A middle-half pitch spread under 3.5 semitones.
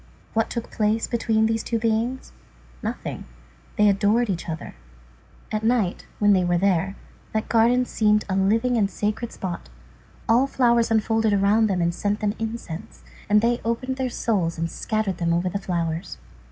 Yes: average, 3.1 semitones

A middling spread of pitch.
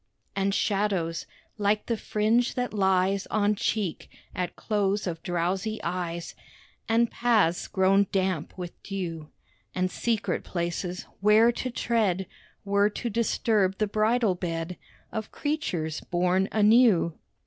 Yes: average, 3.2 semitones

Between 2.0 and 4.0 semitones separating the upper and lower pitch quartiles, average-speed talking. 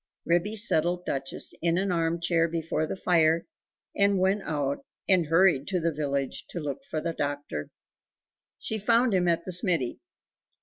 Yes: average, 3.2 semitones; average, 160 wpm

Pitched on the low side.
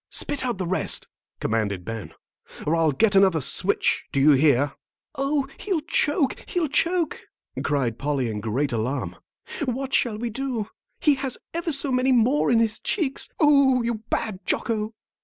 No: high, 225 Hz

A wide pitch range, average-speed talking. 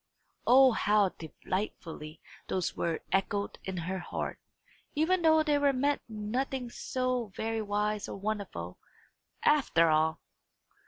No: wide, 5.9 semitones; slow, 115 wpm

